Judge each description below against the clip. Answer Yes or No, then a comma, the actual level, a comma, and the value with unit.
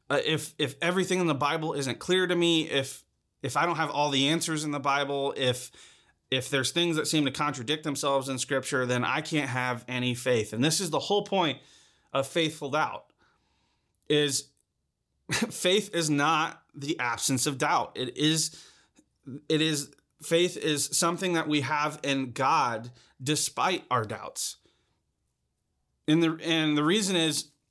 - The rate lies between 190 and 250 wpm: No, average, 165 wpm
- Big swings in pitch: No, average, 3.0 semitones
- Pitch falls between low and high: Yes, medium, 150 Hz